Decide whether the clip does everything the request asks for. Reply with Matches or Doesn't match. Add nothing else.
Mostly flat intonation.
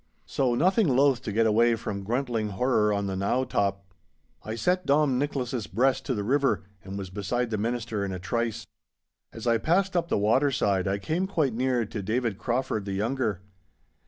Doesn't match